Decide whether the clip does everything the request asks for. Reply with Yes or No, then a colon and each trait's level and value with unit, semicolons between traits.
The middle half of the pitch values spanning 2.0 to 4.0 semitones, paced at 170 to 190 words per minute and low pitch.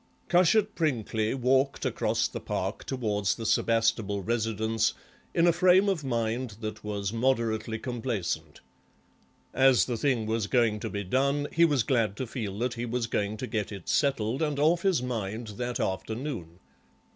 No: average, 3.6 semitones; average, 160 wpm; low, 115 Hz